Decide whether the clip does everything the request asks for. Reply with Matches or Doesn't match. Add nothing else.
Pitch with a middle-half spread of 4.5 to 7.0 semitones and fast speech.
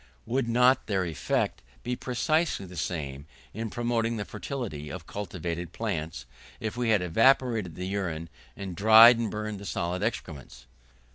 Doesn't match